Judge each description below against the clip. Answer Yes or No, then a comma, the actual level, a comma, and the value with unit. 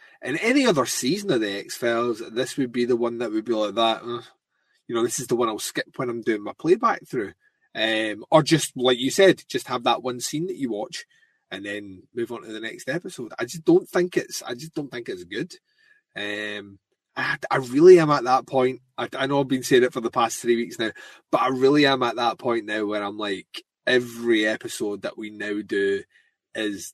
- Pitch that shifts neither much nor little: No, wide, 6.7 semitones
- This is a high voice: No, low, 125 Hz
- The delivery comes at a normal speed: No, fast, 235 wpm